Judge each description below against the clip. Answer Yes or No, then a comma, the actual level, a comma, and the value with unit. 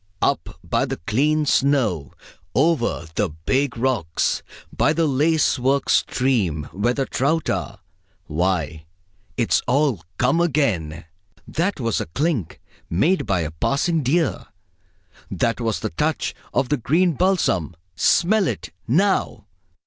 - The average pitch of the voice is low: Yes, low, 130 Hz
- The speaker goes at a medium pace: No, slow, 130 wpm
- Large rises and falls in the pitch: Yes, wide, 8.4 semitones